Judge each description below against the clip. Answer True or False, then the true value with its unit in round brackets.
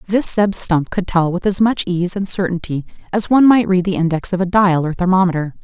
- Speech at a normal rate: False (235 wpm)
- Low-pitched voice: False (185 Hz)